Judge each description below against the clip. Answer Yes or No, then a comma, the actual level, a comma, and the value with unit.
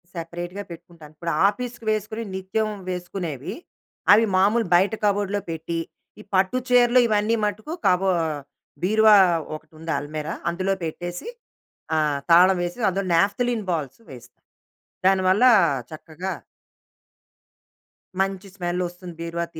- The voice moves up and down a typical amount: Yes, average, 3.7 semitones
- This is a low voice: No, medium, 185 Hz